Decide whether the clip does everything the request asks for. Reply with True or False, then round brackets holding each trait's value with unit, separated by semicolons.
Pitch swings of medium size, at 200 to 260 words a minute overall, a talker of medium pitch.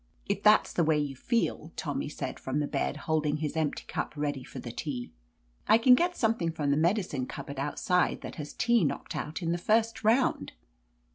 False (6.6 semitones; 205 wpm; 160 Hz)